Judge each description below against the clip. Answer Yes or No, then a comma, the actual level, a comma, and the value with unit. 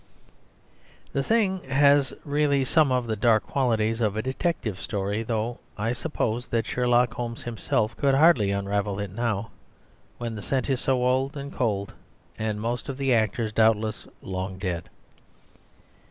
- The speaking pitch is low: Yes, low, 115 Hz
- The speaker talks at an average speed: Yes, average, 155 wpm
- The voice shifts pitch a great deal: No, average, 3.8 semitones